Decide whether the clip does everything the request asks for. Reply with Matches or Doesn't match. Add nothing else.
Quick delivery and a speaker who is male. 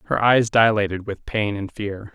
Doesn't match